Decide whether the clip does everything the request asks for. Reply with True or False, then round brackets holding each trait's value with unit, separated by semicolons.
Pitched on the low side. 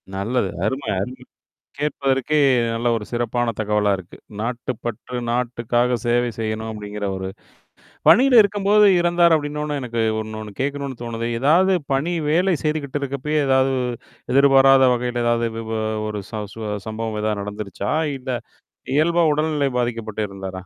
True (125 Hz)